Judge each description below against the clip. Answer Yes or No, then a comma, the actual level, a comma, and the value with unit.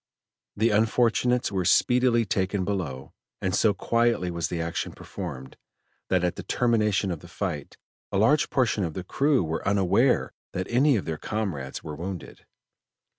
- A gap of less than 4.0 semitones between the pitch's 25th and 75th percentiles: No, average, 5.0 semitones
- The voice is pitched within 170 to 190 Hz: No, low, 100 Hz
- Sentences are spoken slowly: No, average, 160 wpm